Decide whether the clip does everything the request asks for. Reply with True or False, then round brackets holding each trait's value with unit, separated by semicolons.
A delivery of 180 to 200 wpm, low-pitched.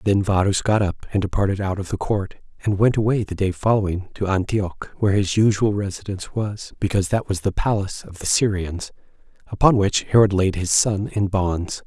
True (195 wpm; 100 Hz)